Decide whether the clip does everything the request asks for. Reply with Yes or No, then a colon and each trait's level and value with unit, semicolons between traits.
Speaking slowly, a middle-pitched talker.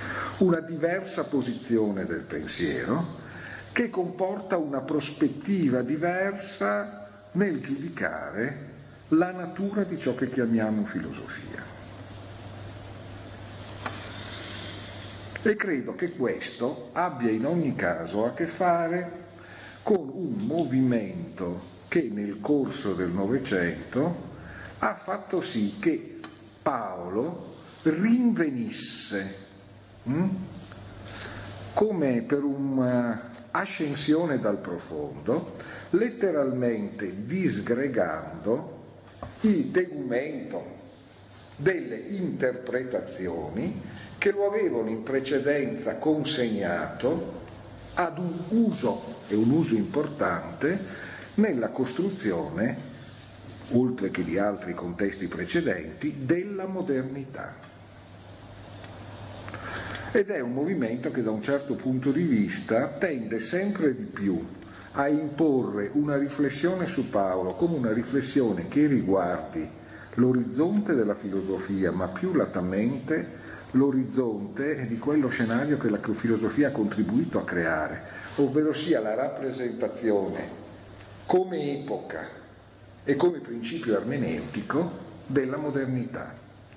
No: slow, 90 wpm; low, 120 Hz